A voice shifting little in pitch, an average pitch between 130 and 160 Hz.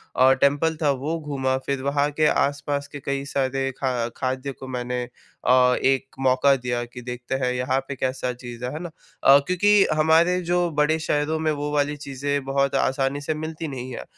Yes: narrow, 2.2 semitones; medium, 140 Hz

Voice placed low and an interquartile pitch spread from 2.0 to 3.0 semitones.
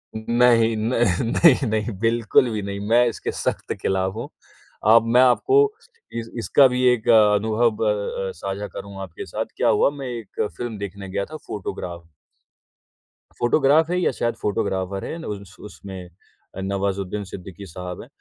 No: low, 110 Hz; average, 3.4 semitones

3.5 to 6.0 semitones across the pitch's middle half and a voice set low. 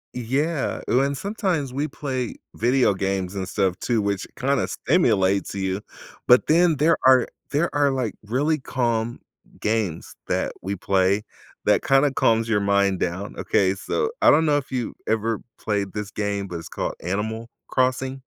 Yes: wide, 5.4 semitones; low, 115 Hz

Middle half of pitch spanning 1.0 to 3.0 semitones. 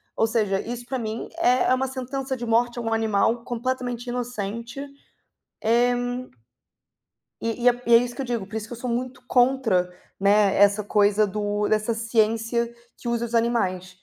Yes: narrow, 2.4 semitones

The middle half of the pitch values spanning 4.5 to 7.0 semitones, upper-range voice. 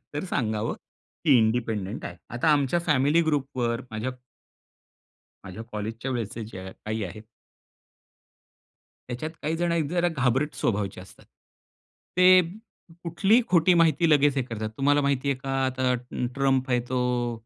No: average, 5.2 semitones; low, 130 Hz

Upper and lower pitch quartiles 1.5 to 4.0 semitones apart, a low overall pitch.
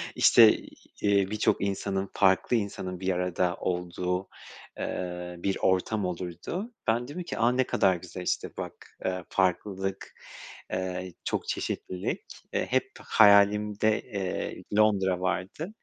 Yes: narrow, 2.4 semitones; very low, 95 Hz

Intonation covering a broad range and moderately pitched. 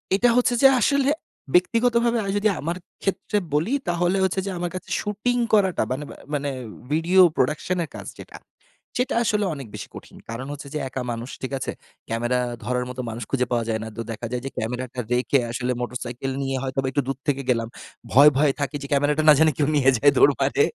Yes: wide, 6.7 semitones; medium, 145 Hz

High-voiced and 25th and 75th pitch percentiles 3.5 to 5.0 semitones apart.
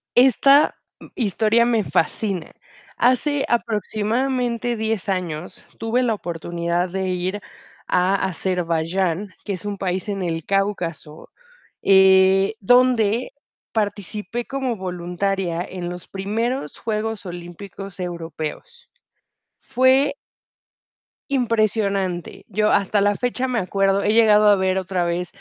Yes: high, 200 Hz; average, 3.9 semitones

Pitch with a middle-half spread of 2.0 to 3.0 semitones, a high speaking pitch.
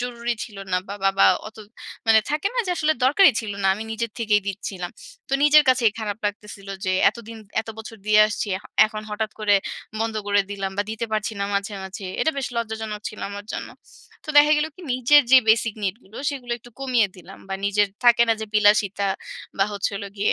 Yes: average, 2.7 semitones; high, 215 Hz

